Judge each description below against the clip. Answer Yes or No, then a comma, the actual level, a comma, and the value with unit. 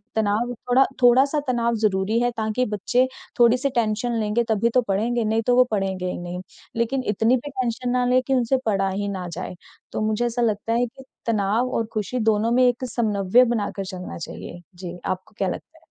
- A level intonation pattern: No, average, 3.4 semitones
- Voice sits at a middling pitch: No, high, 230 Hz